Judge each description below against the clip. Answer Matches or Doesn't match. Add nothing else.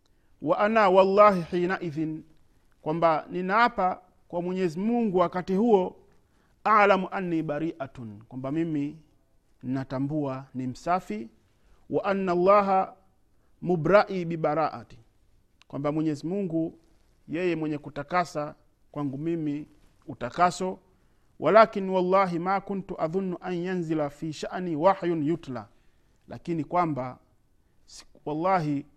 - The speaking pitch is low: Doesn't match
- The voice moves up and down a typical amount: Matches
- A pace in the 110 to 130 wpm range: Doesn't match